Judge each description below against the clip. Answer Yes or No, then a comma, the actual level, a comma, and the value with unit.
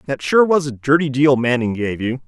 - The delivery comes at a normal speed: No, fast, 235 wpm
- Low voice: Yes, low, 130 Hz